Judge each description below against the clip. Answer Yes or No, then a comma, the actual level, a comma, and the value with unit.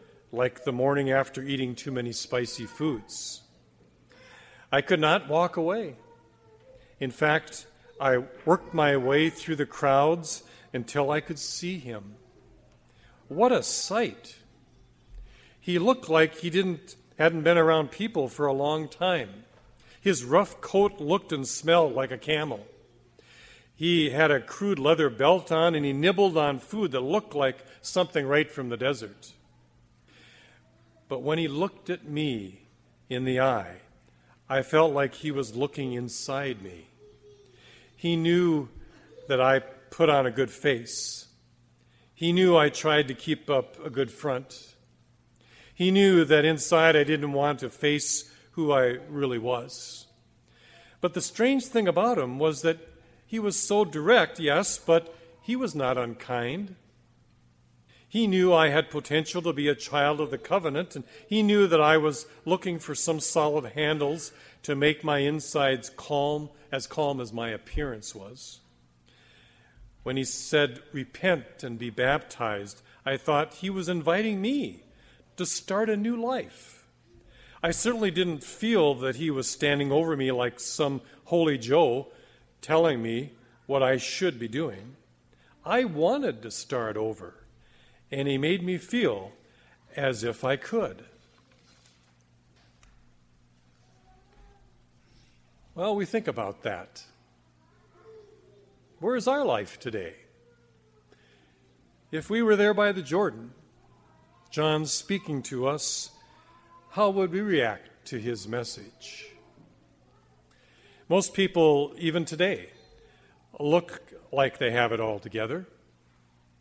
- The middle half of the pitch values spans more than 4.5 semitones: Yes, wide, 5.4 semitones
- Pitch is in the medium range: Yes, medium, 145 Hz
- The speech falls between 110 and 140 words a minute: Yes, slow, 135 wpm